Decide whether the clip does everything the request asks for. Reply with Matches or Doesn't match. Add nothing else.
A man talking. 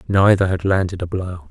Matches